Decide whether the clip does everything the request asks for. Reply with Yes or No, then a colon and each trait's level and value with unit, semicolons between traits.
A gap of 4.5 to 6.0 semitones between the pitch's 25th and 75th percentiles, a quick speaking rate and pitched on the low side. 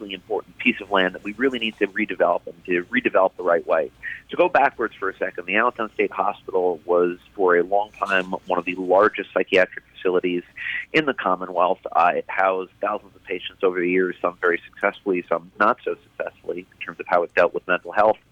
No: average, 4.0 semitones; fast, 215 wpm; very low, 95 Hz